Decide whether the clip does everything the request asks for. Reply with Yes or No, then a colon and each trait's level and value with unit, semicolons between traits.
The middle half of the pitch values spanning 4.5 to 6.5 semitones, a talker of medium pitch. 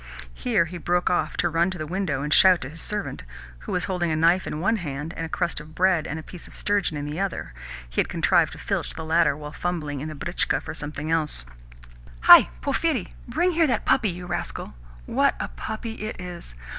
No: average, 3.3 semitones; medium, 165 Hz